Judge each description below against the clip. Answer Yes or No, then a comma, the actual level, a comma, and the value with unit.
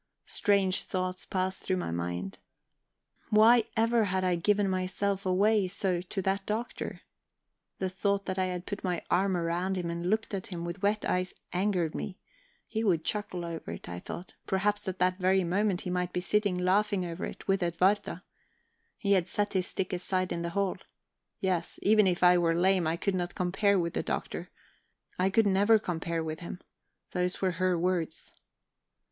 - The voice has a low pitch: No, medium, 185 Hz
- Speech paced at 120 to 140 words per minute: No, average, 185 wpm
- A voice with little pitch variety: Yes, narrow, 2.1 semitones